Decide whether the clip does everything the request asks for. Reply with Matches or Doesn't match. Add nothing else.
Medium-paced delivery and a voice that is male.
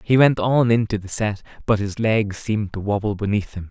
Doesn't match